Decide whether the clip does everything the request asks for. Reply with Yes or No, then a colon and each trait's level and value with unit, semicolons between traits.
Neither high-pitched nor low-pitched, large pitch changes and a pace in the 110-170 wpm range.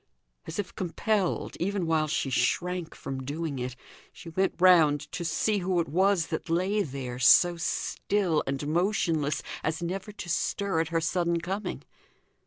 No: medium, 170 Hz; average, 3.2 semitones; average, 160 wpm